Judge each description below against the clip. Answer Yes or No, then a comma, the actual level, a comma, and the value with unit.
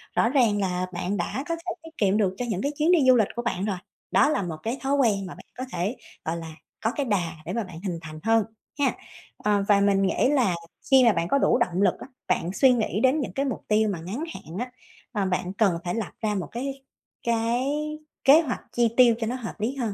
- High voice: Yes, high, 220 Hz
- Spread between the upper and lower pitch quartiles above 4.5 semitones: Yes, average, 5.2 semitones